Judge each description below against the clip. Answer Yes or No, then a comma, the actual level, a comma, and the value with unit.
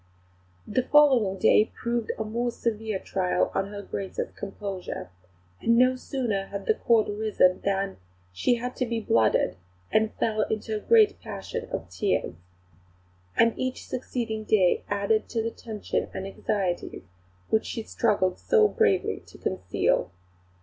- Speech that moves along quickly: No, average, 150 wpm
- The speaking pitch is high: Yes, high, 220 Hz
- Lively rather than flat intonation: No, average, 3.4 semitones